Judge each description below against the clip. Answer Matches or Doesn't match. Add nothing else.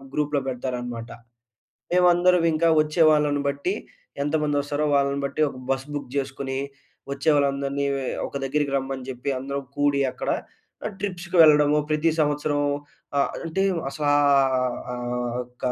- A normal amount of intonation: Doesn't match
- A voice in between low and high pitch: Matches